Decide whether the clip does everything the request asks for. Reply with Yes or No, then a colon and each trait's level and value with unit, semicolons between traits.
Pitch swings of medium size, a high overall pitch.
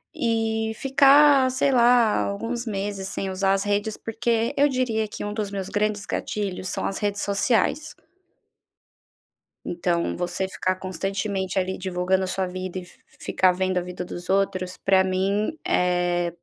Yes: average, 3.0 semitones; high, 195 Hz